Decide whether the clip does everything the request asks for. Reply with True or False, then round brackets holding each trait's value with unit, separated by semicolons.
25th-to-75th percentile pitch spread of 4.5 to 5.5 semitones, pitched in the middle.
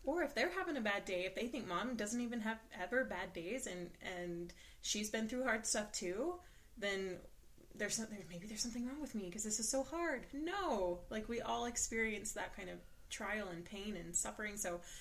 False (4.9 semitones; 210 Hz)